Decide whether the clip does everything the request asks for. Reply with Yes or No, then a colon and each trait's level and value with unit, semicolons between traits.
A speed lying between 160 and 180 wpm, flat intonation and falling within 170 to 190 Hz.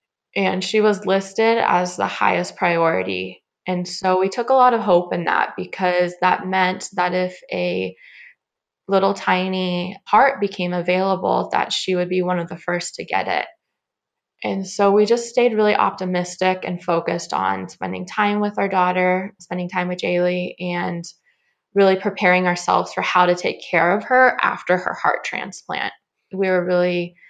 Yes: average, 170 wpm; narrow, 1.9 semitones; medium, 185 Hz